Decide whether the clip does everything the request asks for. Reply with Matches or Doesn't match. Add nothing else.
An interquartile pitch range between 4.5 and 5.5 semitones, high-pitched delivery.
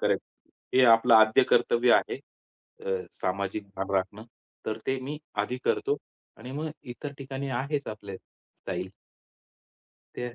Doesn't match